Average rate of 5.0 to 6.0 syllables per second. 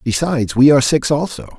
No: 6.4 syllables/s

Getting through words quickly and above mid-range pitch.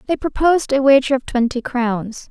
No: average, 180 wpm; very high, 260 Hz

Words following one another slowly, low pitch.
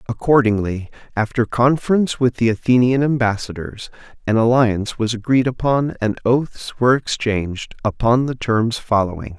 Yes: slow, 130 wpm; low, 115 Hz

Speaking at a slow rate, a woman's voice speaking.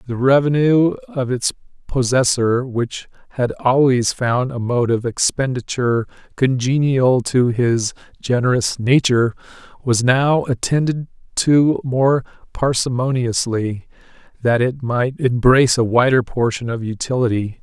No: slow, 110 wpm; male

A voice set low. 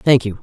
Yes: low, 120 Hz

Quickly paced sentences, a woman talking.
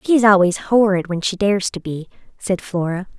No: average, 190 wpm; female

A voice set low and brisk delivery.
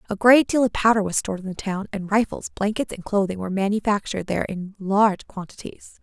No: high, 205 Hz; fast, 210 wpm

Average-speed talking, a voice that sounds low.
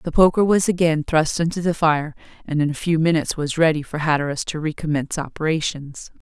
No: average, 195 wpm; medium, 160 Hz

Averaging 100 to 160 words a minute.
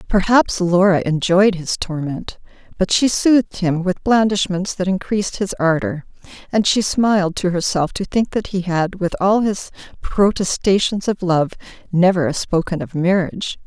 Yes: average, 155 wpm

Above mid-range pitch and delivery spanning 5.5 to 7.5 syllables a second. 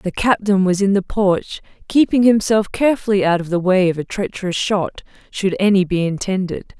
No: high, 195 Hz; 5.1 syllables/s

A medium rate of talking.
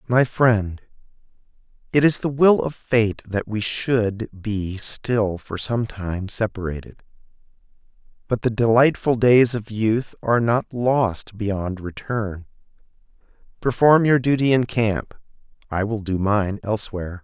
No: slow, 130 wpm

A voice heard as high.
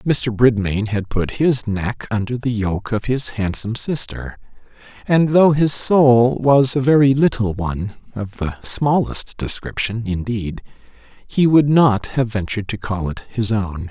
No: low, 115 Hz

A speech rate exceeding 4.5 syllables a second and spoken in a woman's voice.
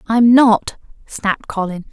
No: 4.1 syllables/s; female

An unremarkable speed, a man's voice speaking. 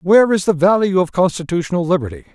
Yes: average, 180 wpm; male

